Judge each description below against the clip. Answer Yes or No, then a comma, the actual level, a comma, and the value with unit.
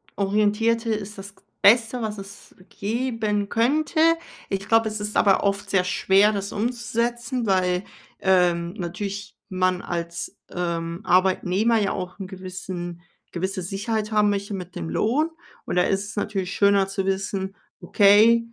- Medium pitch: No, high, 200 Hz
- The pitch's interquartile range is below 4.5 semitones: Yes, narrow, 2.6 semitones